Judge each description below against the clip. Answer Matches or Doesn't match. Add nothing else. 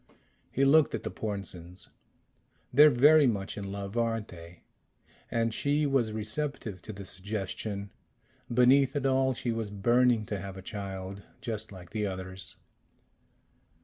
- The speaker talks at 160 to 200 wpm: Doesn't match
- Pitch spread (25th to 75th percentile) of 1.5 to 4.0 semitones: Doesn't match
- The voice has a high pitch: Doesn't match